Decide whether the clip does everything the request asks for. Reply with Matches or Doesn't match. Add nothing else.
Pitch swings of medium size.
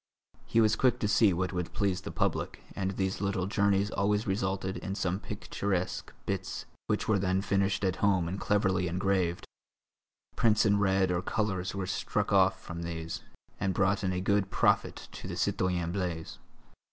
Doesn't match